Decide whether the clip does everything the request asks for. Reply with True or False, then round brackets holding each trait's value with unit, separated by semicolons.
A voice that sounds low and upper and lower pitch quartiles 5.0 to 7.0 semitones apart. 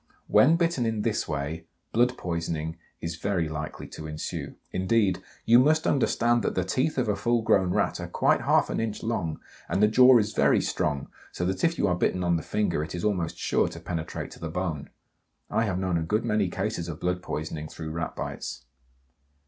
True (90 Hz; 5.5 semitones)